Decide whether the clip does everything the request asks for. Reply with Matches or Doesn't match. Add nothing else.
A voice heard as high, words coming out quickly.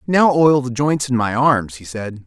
Doesn't match